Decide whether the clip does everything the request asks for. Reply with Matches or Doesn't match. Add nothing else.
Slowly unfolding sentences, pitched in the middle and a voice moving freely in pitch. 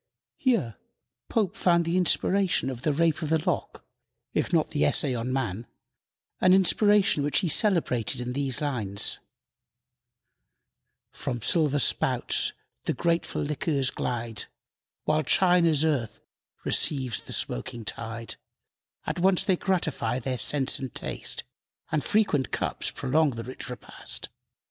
Matches